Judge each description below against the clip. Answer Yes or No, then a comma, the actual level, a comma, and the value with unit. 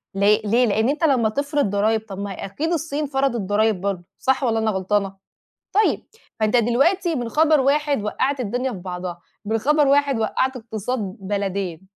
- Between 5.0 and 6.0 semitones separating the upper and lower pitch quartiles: Yes, wide, 5.6 semitones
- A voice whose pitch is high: Yes, high, 225 Hz